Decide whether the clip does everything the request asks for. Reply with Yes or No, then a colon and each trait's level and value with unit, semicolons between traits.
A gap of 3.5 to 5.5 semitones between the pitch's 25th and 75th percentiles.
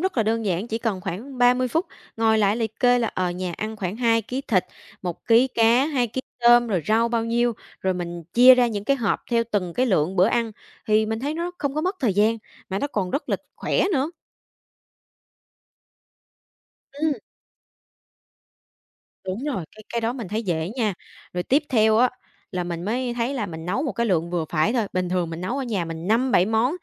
Yes: average, 4.9 semitones